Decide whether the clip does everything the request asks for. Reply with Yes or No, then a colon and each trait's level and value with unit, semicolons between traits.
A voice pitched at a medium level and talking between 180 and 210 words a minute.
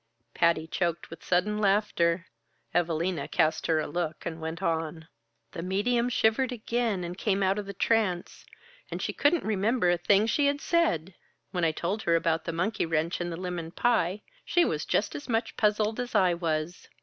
Yes: medium, 180 Hz; average, 185 wpm